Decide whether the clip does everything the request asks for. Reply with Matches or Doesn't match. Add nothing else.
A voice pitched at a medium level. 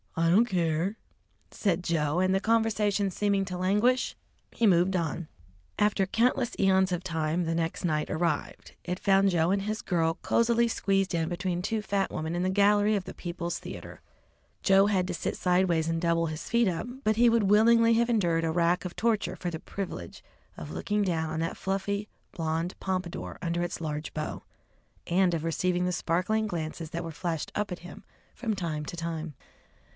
Matches